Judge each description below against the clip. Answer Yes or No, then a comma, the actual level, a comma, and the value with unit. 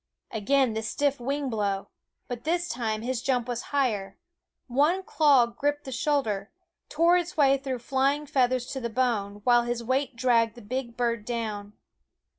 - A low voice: No, high, 245 Hz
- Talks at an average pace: Yes, average, 165 wpm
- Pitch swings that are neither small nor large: Yes, average, 3.4 semitones